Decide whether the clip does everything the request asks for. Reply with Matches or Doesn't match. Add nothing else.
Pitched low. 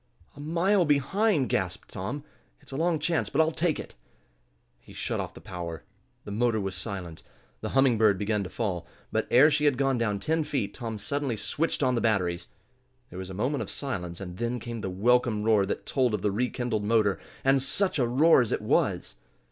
Matches